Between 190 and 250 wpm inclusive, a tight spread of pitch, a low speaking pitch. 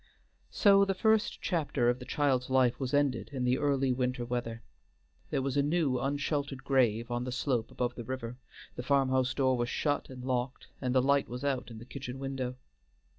Yes: average, 200 wpm; narrow, 2.1 semitones; low, 130 Hz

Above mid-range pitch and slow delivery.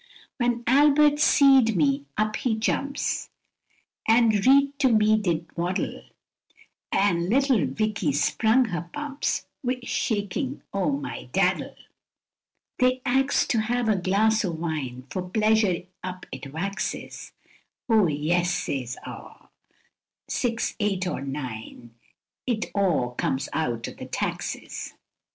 Yes: high, 210 Hz; slow, 120 wpm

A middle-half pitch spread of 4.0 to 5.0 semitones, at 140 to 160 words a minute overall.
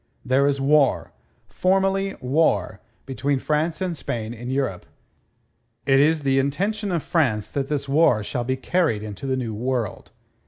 Yes: average, 4.4 semitones; average, 155 wpm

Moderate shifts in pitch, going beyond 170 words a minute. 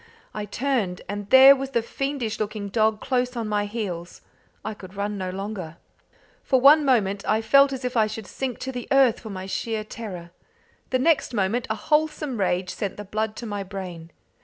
Yes: average, 4.3 semitones; average, 190 wpm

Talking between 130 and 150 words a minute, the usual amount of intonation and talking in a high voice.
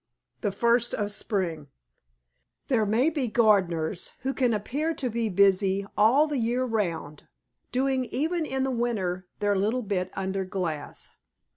Yes: average, 145 wpm; average, 5.0 semitones; high, 215 Hz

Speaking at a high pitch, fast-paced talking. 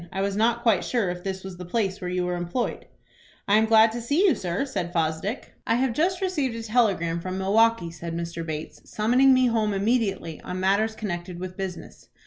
Yes: high, 200 Hz; fast, 210 wpm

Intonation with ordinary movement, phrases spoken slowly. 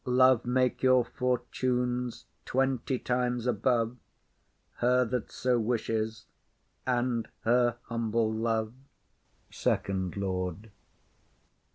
No: narrow, 2.1 semitones; slow, 85 wpm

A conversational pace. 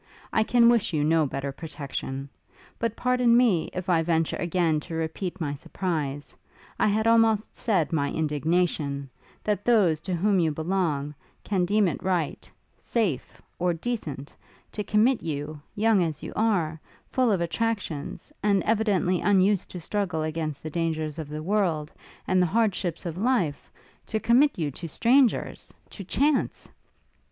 Yes: average, 155 wpm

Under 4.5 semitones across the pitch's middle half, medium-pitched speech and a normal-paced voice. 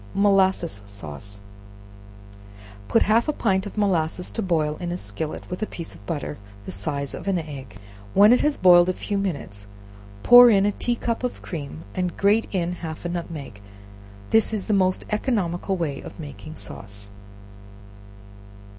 No: average, 5.2 semitones; medium, 175 Hz; average, 165 wpm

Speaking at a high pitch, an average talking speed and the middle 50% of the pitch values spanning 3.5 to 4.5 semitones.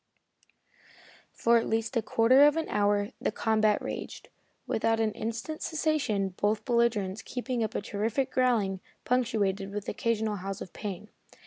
No: high, 220 Hz; average, 145 wpm; narrow, 2.6 semitones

